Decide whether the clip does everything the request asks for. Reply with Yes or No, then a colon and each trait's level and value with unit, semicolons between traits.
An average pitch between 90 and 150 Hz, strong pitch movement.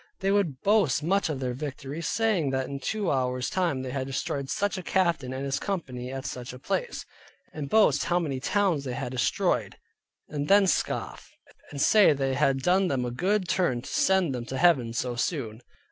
Yes: medium, 140 Hz; wide, 6.1 semitones